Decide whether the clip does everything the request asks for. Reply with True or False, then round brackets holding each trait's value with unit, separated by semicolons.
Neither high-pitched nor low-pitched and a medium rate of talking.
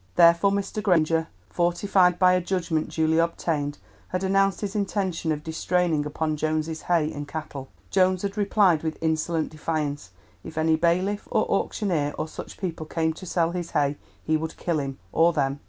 True (165 Hz; 170 wpm)